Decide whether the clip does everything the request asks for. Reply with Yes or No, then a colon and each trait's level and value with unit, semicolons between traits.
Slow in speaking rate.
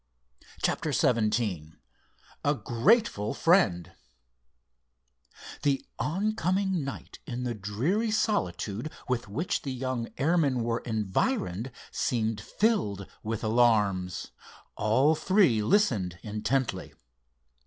Yes: slow, 90 wpm